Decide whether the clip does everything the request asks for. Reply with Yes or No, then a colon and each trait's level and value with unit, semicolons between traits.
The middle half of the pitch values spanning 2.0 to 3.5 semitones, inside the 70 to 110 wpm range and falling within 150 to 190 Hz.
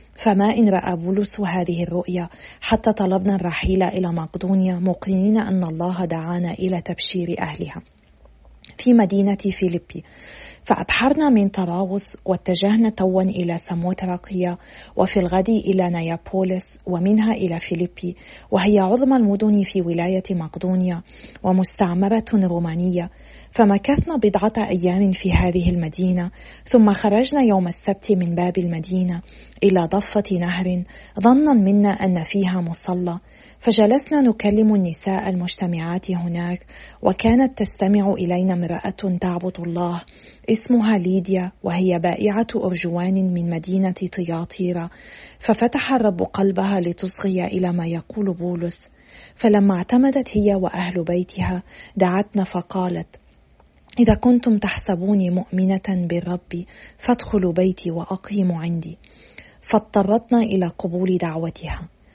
Yes: narrow, 2.5 semitones; average, 105 wpm; medium, 185 Hz